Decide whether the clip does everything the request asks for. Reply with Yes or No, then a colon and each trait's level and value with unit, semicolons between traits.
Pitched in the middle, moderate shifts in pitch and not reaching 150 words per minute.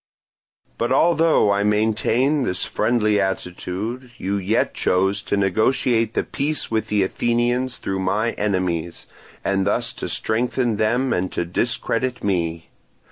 No: low, 110 Hz; average, 4.0 semitones; slow, 135 wpm